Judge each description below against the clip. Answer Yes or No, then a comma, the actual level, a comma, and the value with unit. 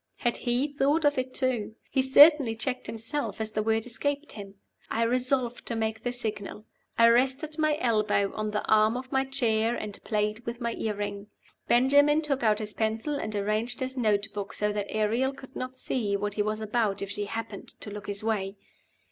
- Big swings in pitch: No, average, 3.5 semitones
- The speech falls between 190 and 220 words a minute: Yes, average, 200 wpm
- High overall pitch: Yes, high, 225 Hz